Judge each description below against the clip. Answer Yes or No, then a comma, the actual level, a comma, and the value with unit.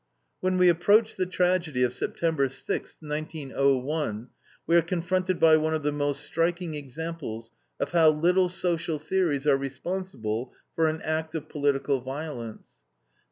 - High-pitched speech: No, medium, 155 Hz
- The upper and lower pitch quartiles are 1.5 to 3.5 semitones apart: No, average, 3.9 semitones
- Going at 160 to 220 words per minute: No, average, 145 wpm